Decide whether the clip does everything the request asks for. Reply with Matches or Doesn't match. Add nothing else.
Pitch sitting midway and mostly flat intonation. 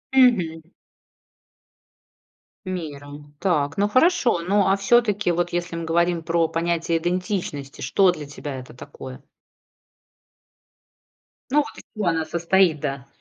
Doesn't match